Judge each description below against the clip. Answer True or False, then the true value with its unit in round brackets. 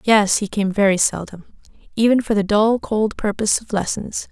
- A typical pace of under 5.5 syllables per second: True (5.1 syllables/s)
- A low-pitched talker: False (210 Hz)